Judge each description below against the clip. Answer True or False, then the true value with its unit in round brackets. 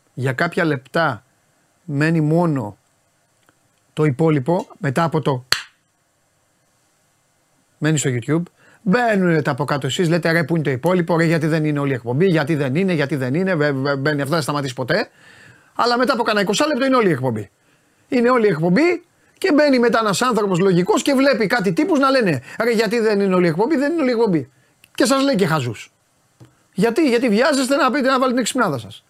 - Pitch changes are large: True (8.3 semitones)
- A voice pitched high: False (170 Hz)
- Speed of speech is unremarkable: False (200 wpm)